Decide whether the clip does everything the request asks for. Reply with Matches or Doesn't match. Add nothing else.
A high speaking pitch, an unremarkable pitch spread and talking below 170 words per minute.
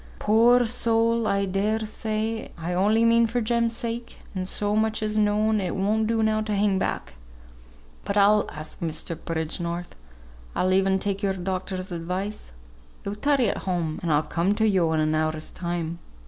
Doesn't match